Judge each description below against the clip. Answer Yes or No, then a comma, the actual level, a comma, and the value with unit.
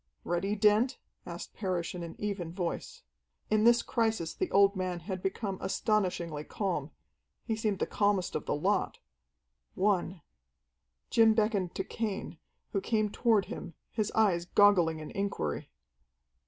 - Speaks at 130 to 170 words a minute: Yes, average, 140 wpm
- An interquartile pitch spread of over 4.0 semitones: No, average, 3.5 semitones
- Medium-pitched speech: No, high, 195 Hz